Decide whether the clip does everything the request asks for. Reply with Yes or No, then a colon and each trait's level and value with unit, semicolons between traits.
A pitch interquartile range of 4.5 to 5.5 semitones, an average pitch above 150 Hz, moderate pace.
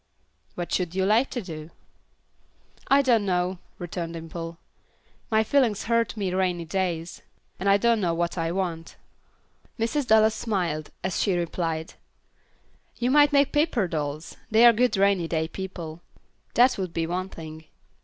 Yes: average, 4.9 semitones; medium, 185 Hz; average, 155 wpm